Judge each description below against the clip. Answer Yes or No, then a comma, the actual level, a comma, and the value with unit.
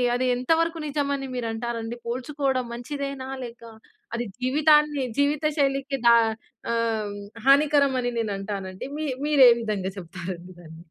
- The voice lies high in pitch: Yes, very high, 255 Hz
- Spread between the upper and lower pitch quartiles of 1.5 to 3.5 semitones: No, average, 4.0 semitones